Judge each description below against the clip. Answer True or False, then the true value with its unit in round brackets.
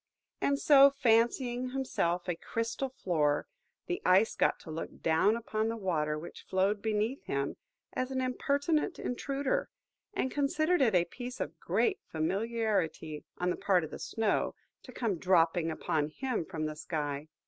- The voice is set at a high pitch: True (215 Hz)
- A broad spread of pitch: True (7.7 semitones)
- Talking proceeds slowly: False (160 wpm)